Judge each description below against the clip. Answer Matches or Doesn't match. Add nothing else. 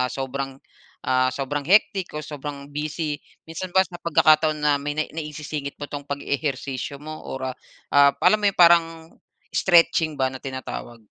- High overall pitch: Doesn't match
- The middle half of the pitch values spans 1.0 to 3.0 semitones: Matches